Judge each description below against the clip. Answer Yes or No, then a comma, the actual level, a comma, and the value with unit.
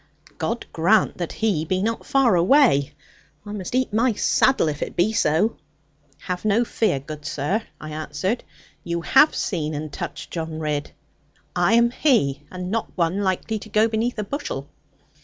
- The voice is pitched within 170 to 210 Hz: Yes, high, 190 Hz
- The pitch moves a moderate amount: No, wide, 6.3 semitones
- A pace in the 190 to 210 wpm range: No, average, 170 wpm